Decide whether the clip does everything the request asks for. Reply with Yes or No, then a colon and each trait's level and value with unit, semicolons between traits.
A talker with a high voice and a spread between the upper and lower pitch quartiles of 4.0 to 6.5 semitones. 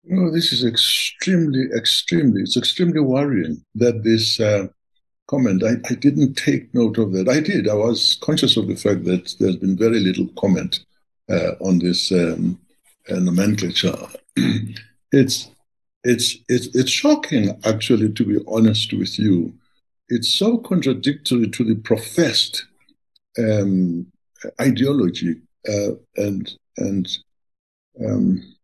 No: low, 115 Hz; average, 4.6 semitones